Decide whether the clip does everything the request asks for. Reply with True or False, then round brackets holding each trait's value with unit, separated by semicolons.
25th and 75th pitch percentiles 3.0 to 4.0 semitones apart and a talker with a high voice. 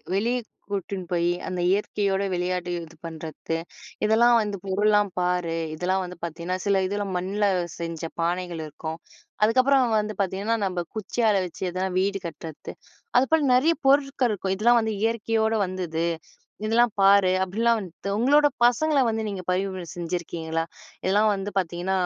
True (3.7 semitones; 195 Hz)